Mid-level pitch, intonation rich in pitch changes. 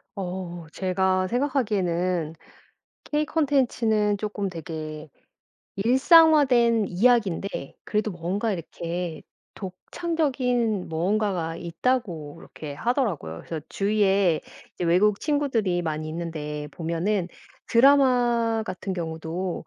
No: high, 195 Hz; wide, 5.7 semitones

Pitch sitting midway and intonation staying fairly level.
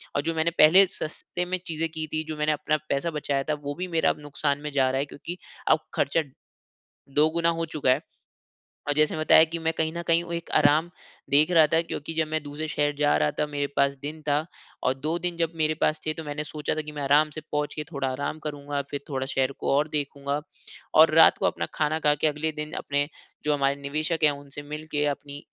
Yes: medium, 150 Hz; narrow, 1.7 semitones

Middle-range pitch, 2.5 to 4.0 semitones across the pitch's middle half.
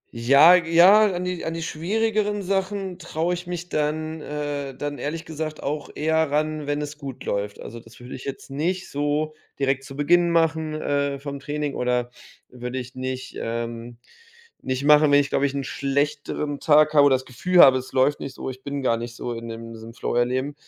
Yes: medium, 145 Hz; average, 3.6 semitones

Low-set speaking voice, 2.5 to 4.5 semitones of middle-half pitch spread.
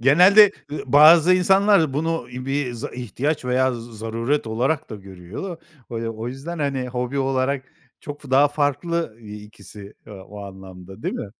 No: low, 130 Hz; average, 5.2 semitones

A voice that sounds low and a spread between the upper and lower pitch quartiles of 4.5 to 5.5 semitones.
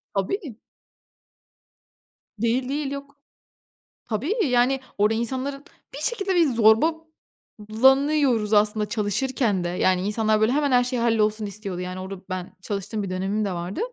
No: high, 225 Hz; average, 4.9 semitones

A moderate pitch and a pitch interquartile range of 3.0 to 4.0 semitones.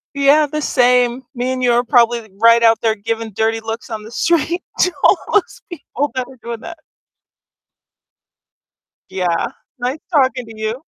No: high, 245 Hz; average, 3.5 semitones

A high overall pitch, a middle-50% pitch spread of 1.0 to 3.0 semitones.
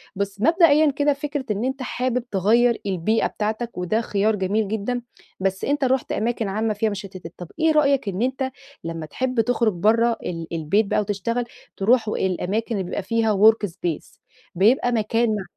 No: high, 220 Hz; average, 4.1 semitones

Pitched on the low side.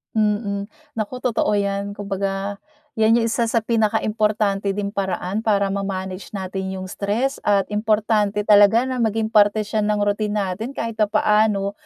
No: high, 210 Hz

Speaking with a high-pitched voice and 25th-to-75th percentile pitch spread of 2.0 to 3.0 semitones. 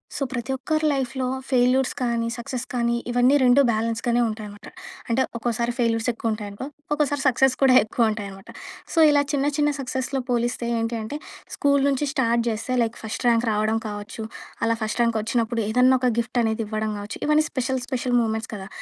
Yes: high, 235 Hz; average, 2.7 semitones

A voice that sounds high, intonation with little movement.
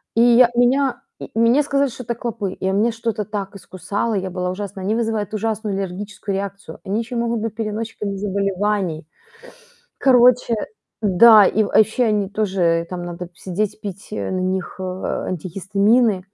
No: high, 205 Hz; average, 3.2 semitones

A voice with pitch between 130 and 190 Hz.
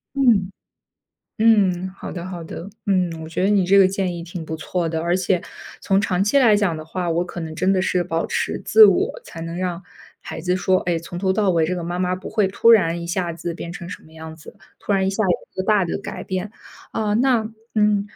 Yes: medium, 185 Hz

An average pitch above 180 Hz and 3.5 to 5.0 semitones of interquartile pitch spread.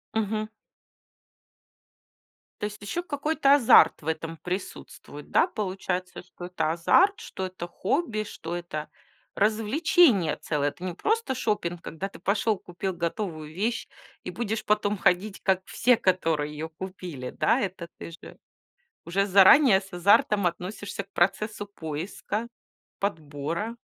Yes: high, 190 Hz; average, 4.0 semitones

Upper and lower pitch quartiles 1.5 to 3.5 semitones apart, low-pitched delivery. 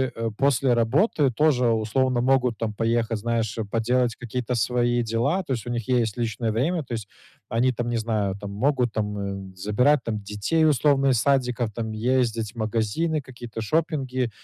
Yes: average, 2.8 semitones; low, 120 Hz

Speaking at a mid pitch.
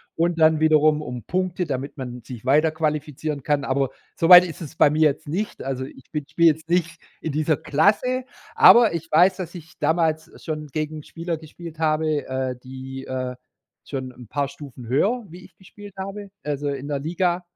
Yes: medium, 155 Hz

